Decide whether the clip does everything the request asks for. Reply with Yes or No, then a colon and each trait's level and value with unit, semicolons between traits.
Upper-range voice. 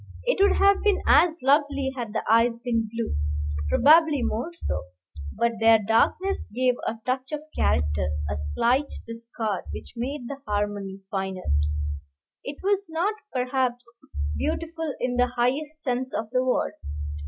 Yes: very high, 250 Hz